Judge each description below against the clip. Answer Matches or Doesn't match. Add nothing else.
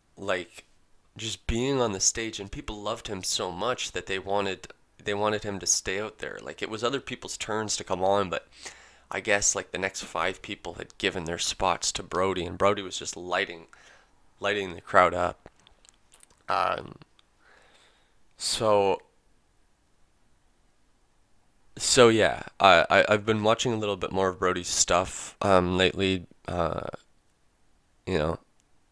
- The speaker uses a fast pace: Doesn't match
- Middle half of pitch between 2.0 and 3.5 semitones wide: Matches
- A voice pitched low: Matches